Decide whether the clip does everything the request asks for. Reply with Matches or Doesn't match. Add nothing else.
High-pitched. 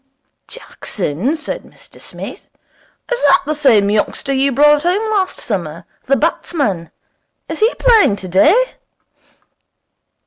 Matches